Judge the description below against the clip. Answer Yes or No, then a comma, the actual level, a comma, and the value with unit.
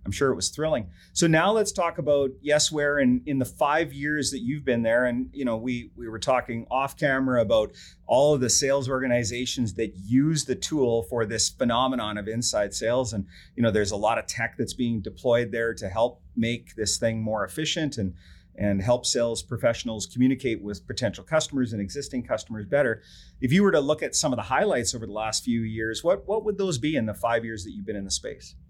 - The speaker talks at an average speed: No, fast, 225 wpm